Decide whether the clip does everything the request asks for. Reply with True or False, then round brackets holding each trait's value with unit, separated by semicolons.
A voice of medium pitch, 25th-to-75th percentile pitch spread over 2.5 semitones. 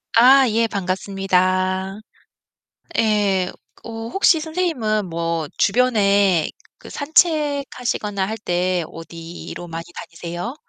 False (200 Hz; 5.2 semitones)